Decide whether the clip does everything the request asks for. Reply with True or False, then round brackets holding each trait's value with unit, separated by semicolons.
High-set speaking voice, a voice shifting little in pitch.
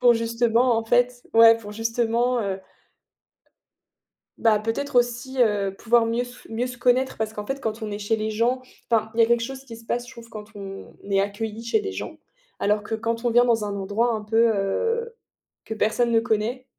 True (230 Hz; 2.1 semitones)